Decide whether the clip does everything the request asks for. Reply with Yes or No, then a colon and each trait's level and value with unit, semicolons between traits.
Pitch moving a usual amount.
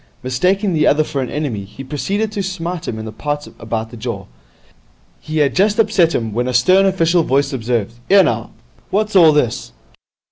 No: wide, 7.5 semitones